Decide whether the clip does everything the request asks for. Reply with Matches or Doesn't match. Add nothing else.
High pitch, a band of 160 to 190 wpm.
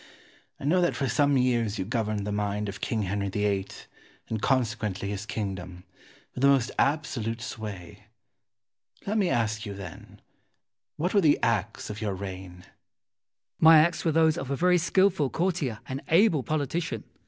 Doesn't match